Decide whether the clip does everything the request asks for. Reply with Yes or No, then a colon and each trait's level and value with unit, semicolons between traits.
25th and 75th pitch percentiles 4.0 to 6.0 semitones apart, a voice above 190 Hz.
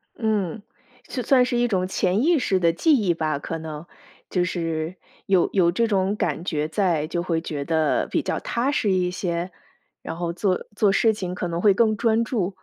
No: average, 4.3 semitones; medium, 185 Hz